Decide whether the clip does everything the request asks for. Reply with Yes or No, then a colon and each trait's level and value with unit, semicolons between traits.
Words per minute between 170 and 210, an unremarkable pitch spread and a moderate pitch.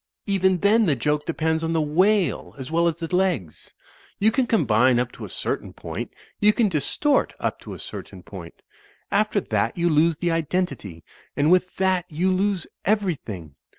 Yes: average, 180 wpm; average, 4.6 semitones; medium, 170 Hz